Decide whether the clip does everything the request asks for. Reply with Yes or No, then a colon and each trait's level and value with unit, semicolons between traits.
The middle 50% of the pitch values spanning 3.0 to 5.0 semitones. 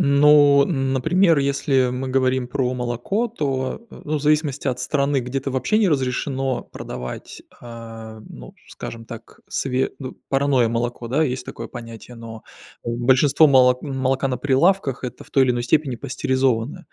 No: narrow, 2.5 semitones